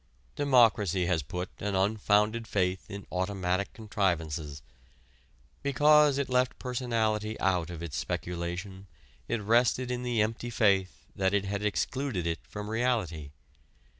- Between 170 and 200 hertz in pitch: No, low, 100 Hz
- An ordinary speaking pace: No, slow, 130 wpm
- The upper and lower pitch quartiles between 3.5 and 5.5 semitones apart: Yes, average, 4.4 semitones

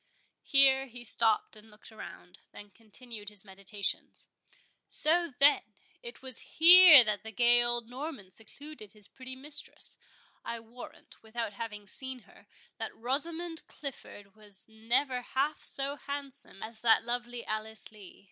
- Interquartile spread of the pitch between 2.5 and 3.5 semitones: No, average, 4.2 semitones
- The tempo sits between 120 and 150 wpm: Yes, slow, 135 wpm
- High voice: Yes, high, 240 Hz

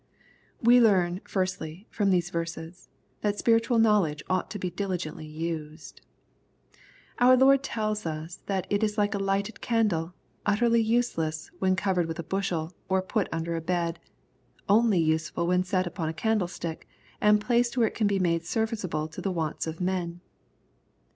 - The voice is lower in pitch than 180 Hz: No, medium, 185 Hz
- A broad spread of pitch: No, average, 4.1 semitones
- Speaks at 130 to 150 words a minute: No, average, 165 wpm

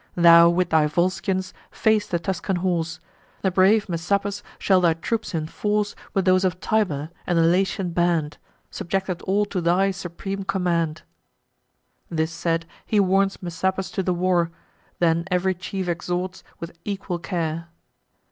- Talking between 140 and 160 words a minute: Yes, average, 145 wpm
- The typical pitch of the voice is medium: Yes, medium, 180 Hz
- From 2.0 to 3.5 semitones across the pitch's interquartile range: Yes, narrow, 2.4 semitones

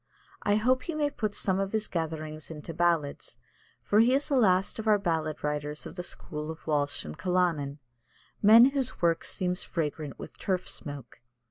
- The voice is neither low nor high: Yes, medium, 175 Hz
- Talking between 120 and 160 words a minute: No, average, 185 wpm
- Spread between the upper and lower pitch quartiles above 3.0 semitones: Yes, wide, 5.6 semitones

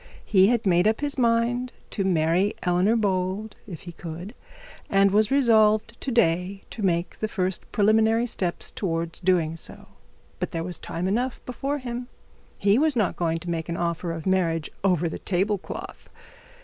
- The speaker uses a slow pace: No, average, 175 wpm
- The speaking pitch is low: No, high, 195 Hz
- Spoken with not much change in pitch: No, average, 4.4 semitones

